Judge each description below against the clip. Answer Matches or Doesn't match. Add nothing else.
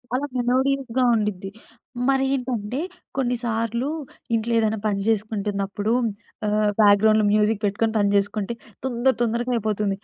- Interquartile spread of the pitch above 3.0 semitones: Doesn't match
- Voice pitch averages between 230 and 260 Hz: Doesn't match